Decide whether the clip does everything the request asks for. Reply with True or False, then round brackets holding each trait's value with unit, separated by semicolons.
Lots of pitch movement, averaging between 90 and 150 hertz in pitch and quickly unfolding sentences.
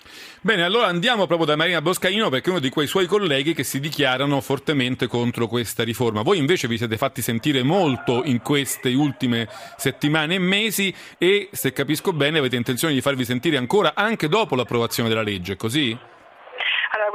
True (5.8 semitones; 140 Hz; 175 wpm)